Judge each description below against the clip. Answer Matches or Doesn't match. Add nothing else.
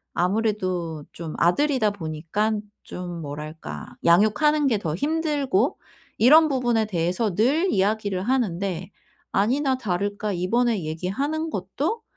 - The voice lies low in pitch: Doesn't match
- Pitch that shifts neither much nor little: Doesn't match